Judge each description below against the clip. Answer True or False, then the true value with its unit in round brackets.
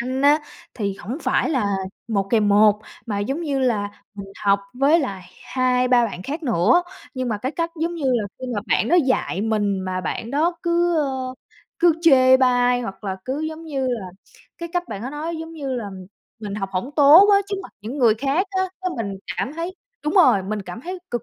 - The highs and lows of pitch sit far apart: True (6.8 semitones)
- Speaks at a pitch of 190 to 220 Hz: False (255 Hz)